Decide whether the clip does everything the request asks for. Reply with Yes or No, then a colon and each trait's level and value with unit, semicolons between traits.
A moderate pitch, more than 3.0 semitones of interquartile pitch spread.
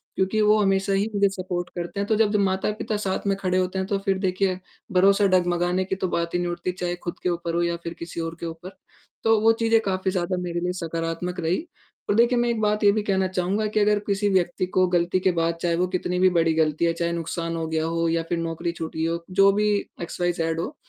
No: medium, 180 Hz; narrow, 2.6 semitones